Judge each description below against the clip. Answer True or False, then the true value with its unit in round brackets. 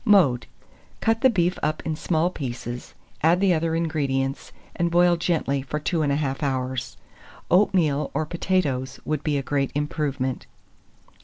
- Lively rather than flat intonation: False (4.0 semitones)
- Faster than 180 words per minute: False (140 wpm)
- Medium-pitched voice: True (150 Hz)